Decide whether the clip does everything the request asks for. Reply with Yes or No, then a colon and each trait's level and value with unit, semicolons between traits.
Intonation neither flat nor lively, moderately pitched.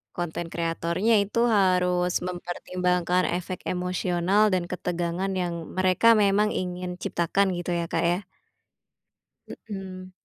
No: narrow, 1.2 semitones; medium, 180 Hz